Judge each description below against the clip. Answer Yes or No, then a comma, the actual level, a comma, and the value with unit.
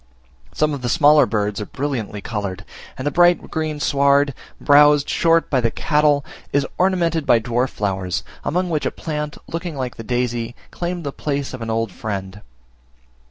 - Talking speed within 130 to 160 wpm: No, average, 170 wpm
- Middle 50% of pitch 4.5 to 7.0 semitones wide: Yes, average, 4.9 semitones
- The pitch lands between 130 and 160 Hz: Yes, medium, 140 Hz